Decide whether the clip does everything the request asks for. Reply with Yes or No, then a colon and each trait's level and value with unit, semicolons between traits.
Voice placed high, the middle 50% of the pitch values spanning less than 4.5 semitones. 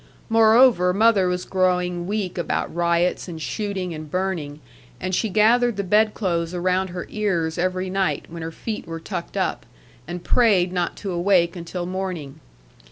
No: medium, 180 Hz; narrow, 2.6 semitones